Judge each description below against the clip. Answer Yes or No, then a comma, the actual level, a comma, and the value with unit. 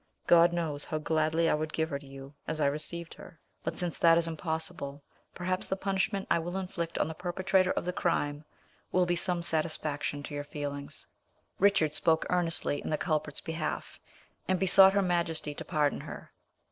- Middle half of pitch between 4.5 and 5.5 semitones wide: No, average, 2.9 semitones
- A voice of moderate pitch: Yes, medium, 165 Hz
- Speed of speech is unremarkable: Yes, average, 185 wpm